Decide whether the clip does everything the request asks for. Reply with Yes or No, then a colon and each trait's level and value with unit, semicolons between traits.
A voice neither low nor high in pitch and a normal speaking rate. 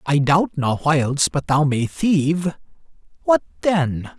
Yes: medium, 155 Hz; average, 145 wpm